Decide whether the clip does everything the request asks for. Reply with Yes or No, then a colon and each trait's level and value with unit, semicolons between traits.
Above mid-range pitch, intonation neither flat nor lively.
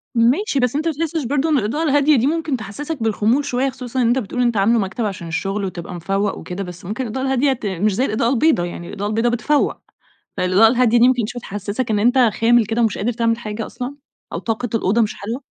Yes: high, 235 Hz; average, 4.2 semitones